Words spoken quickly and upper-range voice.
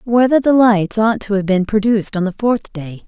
Yes: fast, 235 wpm; high, 210 Hz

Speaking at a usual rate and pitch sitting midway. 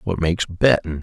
No: average, 175 wpm; very low, 90 Hz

